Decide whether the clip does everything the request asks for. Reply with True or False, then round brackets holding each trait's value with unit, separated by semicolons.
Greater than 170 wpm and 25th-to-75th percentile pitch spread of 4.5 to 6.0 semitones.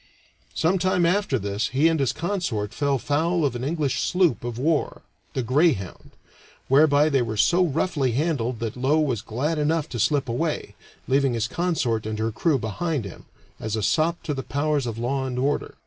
True (190 wpm; 5.2 semitones)